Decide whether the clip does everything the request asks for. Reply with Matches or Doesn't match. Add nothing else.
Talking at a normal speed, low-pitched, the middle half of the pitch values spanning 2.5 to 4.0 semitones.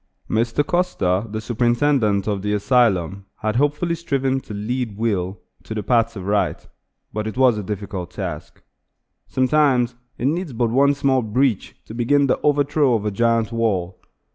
Doesn't match